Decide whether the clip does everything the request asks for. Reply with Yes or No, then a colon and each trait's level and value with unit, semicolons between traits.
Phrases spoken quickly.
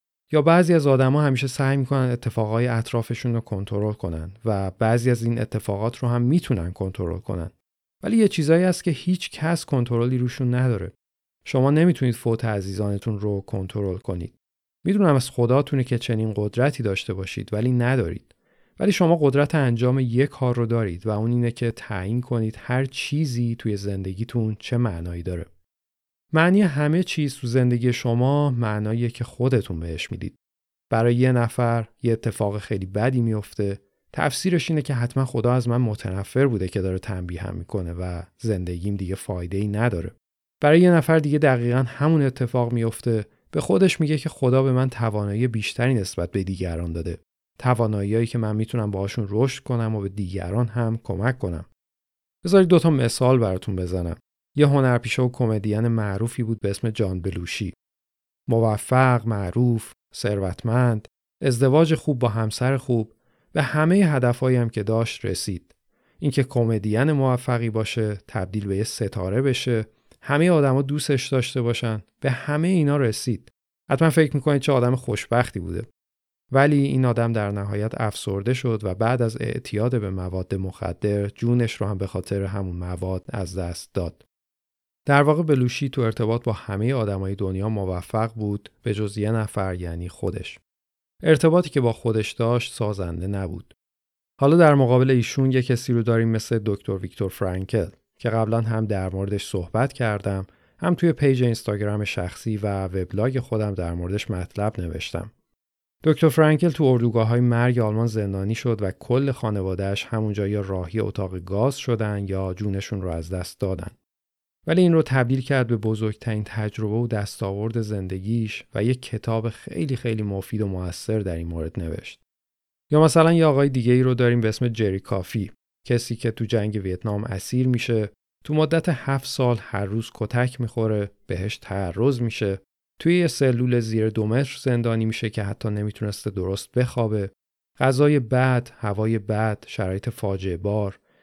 Yes: fast, 160 wpm